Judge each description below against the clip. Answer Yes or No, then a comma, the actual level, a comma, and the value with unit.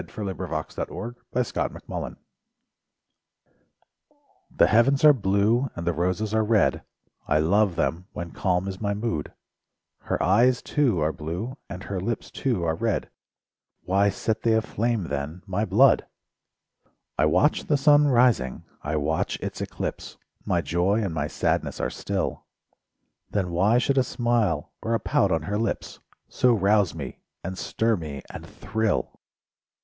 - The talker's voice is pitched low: Yes, low, 100 Hz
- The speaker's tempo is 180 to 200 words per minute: No, average, 155 wpm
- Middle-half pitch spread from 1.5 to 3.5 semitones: No, average, 5.3 semitones